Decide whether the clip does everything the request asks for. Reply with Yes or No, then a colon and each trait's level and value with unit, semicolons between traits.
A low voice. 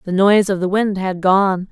No: high, 190 Hz